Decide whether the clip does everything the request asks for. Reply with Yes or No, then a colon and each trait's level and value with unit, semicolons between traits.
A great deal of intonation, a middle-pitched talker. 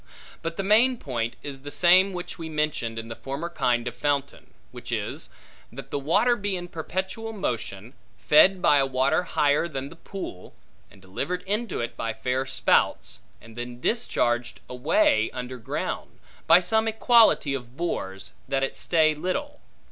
Yes: wide, 7.2 semitones; medium, 150 Hz